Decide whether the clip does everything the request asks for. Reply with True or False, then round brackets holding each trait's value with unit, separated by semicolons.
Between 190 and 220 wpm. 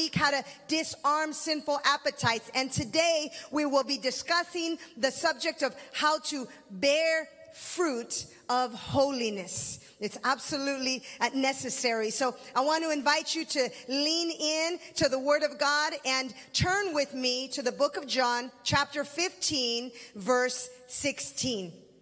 False (135 wpm)